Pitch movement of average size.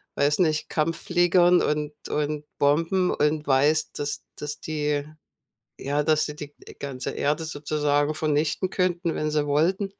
No: narrow, 2.2 semitones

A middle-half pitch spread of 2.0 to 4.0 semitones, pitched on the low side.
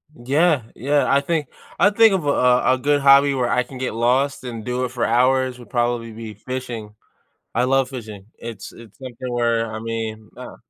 Yes: average, 2.7 semitones; low, 125 Hz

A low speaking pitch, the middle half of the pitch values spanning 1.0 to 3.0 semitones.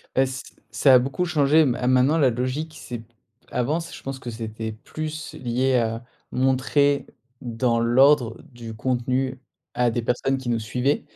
Yes: low, 130 Hz; narrow, 2.6 semitones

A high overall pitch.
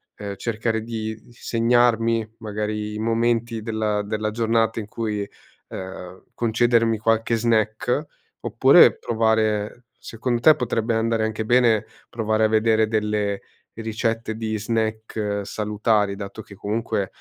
No: low, 110 Hz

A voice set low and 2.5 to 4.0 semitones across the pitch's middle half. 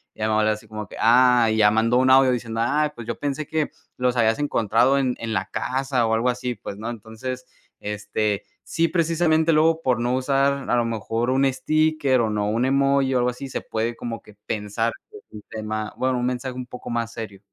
Yes: low, 120 Hz; average, 3.3 semitones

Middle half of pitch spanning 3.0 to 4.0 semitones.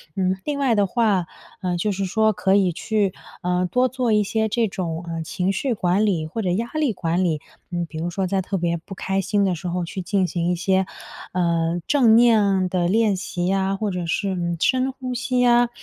Yes: average, 3.7 semitones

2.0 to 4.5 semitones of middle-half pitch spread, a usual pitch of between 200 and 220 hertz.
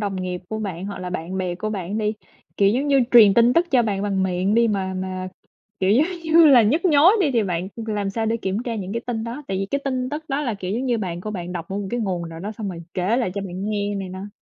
Yes: average, 3.9 semitones; high, 205 Hz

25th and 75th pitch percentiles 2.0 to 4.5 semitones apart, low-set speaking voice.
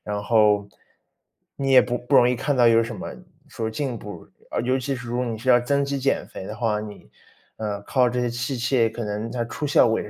Yes: average, 2.7 semitones; low, 120 Hz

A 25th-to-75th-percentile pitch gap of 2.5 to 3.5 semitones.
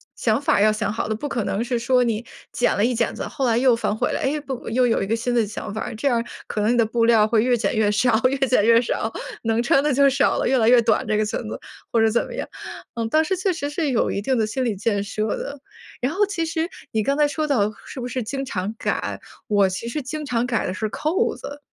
No: average, 4.0 semitones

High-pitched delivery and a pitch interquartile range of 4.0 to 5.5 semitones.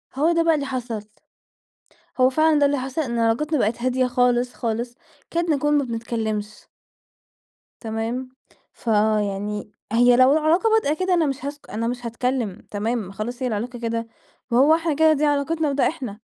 Yes: very high, 250 Hz; average, 4.5 semitones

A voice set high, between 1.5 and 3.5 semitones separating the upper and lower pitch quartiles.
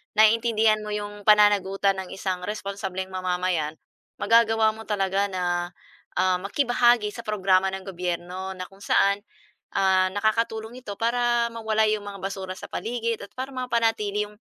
Yes: high, 205 Hz; average, 2.8 semitones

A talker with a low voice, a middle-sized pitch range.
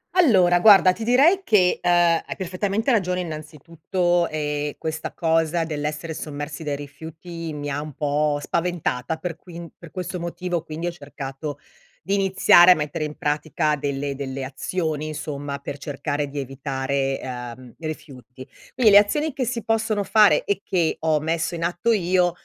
No: medium, 160 Hz; average, 3.7 semitones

